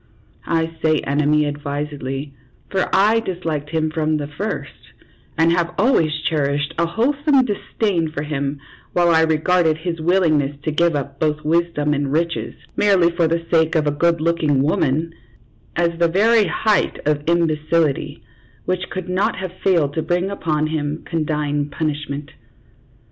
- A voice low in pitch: No, medium, 160 Hz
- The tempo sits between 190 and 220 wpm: No, average, 155 wpm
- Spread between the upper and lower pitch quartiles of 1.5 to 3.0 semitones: Yes, narrow, 2.6 semitones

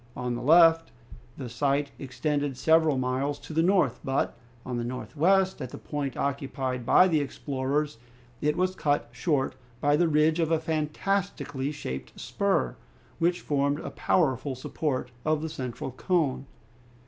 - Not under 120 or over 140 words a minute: No, average, 150 wpm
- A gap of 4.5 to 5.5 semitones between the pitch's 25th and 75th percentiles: No, average, 3.6 semitones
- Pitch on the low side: No, medium, 145 Hz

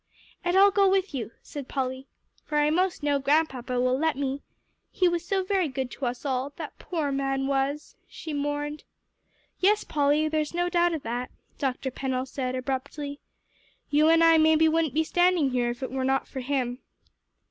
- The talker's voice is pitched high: Yes, very high, 290 Hz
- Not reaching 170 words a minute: No, average, 185 wpm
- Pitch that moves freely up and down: No, average, 3.6 semitones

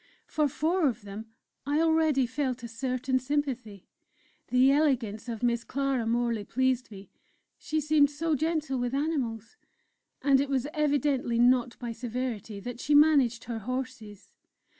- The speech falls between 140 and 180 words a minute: Yes, average, 145 wpm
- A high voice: Yes, very high, 255 Hz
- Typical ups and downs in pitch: Yes, average, 3.6 semitones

